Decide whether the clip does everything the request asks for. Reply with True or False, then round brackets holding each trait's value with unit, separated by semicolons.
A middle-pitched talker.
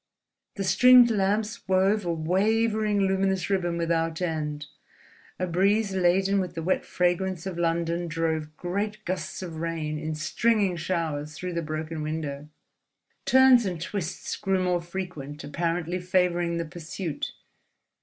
True (175 Hz)